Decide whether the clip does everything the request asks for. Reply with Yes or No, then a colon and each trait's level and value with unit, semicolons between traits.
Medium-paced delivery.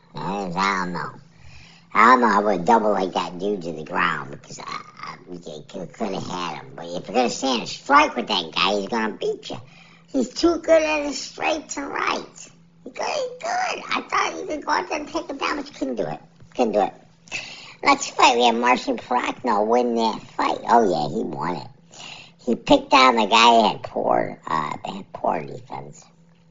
No: fast, 220 wpm